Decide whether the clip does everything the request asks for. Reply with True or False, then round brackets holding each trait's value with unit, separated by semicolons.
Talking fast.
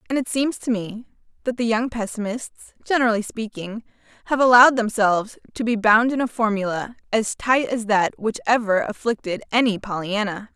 False (165 wpm)